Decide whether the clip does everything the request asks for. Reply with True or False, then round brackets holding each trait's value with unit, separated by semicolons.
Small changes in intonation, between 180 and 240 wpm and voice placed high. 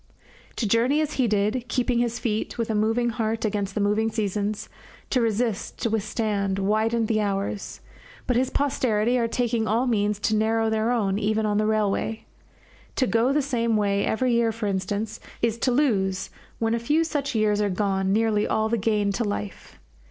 True (2.1 semitones; 190 wpm; 220 Hz)